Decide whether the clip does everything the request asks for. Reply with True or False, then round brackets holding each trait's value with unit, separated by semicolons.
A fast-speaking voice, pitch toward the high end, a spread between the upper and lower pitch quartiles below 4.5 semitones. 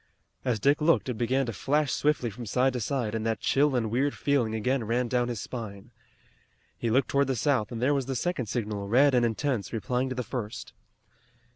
False (215 wpm; 125 Hz; 3.3 semitones)